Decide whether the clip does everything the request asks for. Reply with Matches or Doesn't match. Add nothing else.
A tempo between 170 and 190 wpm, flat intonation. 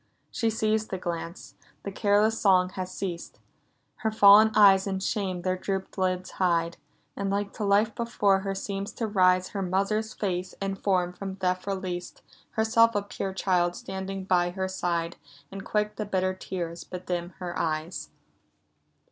Matches